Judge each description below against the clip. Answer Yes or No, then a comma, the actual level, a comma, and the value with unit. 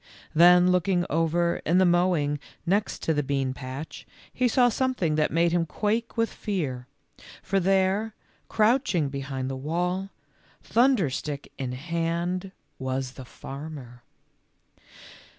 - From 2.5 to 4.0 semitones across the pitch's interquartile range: No, wide, 5.4 semitones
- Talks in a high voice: No, medium, 170 Hz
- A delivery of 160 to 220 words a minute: No, slow, 135 wpm